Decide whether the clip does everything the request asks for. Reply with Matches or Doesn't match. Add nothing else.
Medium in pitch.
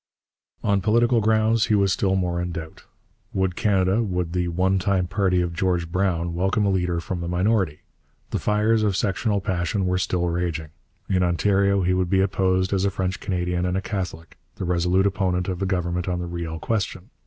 Doesn't match